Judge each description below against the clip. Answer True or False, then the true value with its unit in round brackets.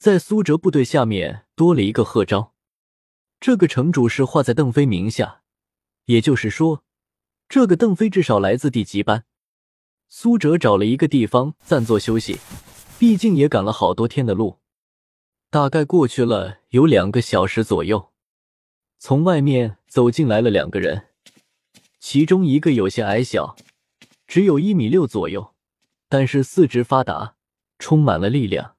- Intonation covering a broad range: True (5.9 semitones)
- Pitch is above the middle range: False (130 Hz)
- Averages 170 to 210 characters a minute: False (225 characters per minute)